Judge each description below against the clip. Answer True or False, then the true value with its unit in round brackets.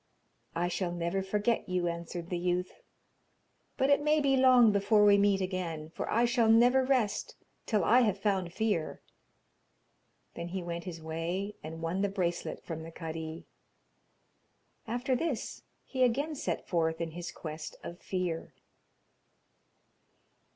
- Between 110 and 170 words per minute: True (145 wpm)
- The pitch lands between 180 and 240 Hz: True (190 Hz)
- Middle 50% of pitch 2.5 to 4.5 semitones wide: False (5.2 semitones)